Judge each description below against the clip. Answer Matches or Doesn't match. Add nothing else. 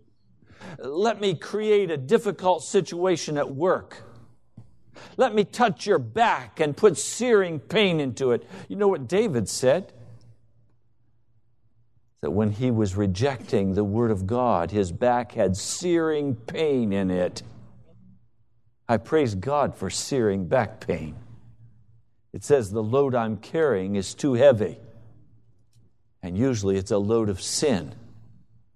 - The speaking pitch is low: Matches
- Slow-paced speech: Matches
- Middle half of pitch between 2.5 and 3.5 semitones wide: Doesn't match